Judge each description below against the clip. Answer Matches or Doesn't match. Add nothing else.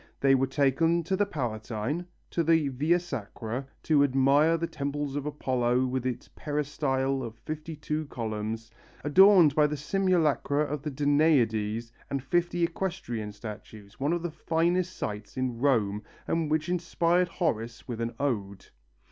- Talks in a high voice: Doesn't match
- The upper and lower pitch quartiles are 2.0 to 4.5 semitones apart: Doesn't match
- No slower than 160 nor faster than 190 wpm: Doesn't match